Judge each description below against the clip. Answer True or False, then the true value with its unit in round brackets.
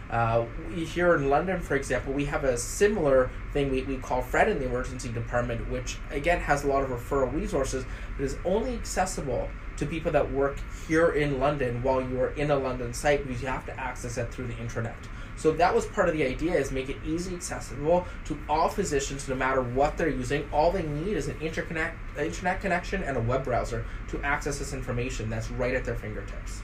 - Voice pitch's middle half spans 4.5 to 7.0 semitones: False (3.5 semitones)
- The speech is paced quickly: True (220 wpm)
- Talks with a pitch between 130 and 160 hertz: True (135 Hz)